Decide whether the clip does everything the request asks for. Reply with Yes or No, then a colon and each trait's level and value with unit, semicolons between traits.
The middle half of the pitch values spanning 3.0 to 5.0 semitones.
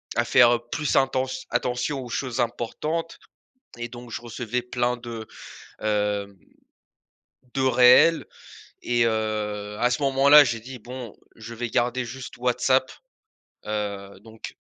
No: narrow, 2.6 semitones